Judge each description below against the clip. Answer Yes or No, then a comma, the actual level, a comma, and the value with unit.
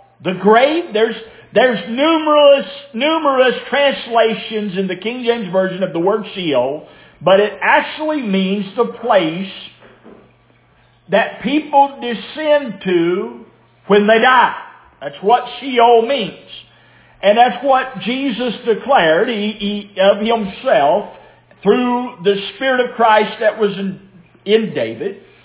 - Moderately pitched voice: No, high, 225 Hz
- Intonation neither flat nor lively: Yes, average, 4.7 semitones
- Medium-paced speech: No, slow, 125 wpm